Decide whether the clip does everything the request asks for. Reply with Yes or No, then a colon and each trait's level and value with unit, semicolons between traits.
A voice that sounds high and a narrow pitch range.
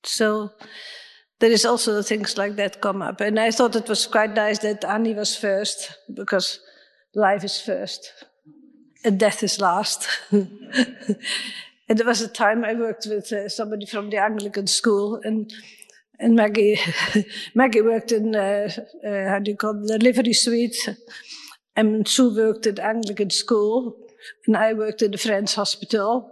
Yes: high, 215 Hz; narrow, 1.8 semitones